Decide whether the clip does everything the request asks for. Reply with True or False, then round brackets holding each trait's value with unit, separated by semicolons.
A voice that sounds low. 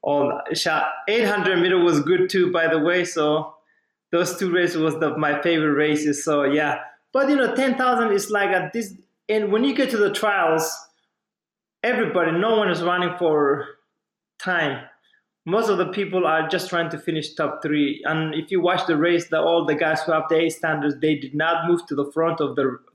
False (170 Hz)